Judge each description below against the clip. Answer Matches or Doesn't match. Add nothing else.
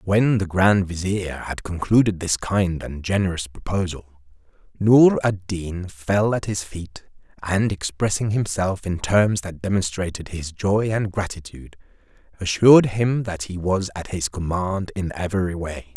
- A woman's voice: Doesn't match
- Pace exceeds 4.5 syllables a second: Doesn't match